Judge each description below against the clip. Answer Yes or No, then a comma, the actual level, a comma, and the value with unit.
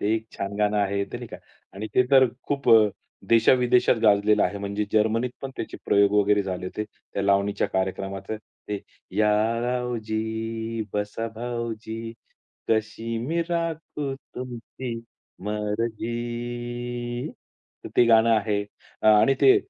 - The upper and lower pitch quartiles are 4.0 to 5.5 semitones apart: No, narrow, 2.6 semitones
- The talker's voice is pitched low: Yes, low, 110 Hz